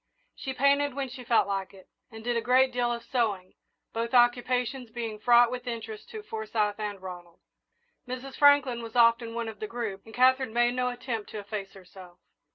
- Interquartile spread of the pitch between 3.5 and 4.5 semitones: No, average, 2.7 semitones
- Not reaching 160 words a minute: No, average, 190 wpm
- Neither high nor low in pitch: No, high, 235 Hz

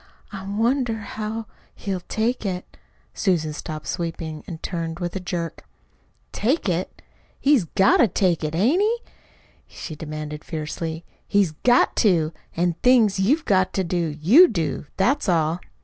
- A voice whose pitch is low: No, medium, 185 Hz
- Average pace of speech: Yes, average, 150 wpm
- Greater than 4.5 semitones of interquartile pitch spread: Yes, average, 5.1 semitones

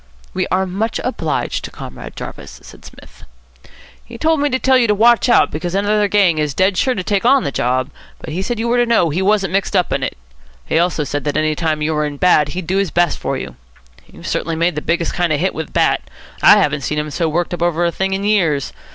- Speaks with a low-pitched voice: No, medium, 175 Hz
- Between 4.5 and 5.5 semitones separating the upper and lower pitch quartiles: Yes, average, 4.9 semitones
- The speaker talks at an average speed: No, fast, 255 wpm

